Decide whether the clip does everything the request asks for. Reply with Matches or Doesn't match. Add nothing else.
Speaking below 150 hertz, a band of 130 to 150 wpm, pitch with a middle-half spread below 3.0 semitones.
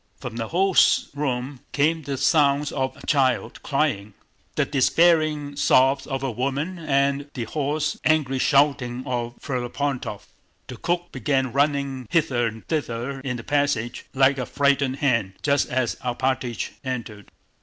Matches